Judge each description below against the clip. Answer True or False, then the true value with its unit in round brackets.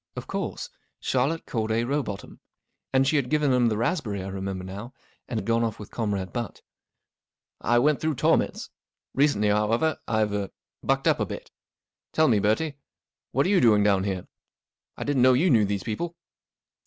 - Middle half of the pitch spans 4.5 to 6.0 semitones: True (5.0 semitones)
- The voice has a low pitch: True (115 Hz)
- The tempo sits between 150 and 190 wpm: True (175 wpm)